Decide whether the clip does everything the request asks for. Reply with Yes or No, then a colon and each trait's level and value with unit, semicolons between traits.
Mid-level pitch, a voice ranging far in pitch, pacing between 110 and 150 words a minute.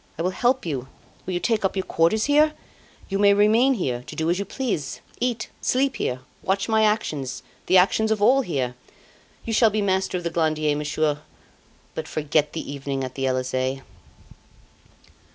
No: medium, 180 Hz; wide, 6.9 semitones; average, 180 wpm